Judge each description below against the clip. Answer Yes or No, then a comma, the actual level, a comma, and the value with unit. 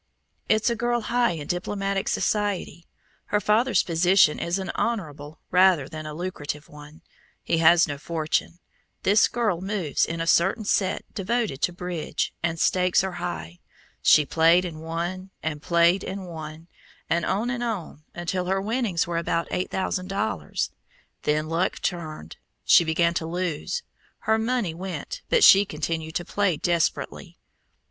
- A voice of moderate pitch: Yes, medium, 175 Hz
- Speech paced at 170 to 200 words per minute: No, average, 155 wpm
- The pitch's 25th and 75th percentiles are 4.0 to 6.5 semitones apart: No, average, 3.6 semitones